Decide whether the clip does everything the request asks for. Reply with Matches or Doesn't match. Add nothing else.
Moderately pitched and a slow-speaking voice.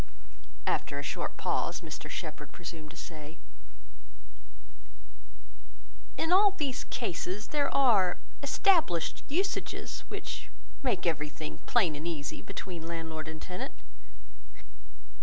Matches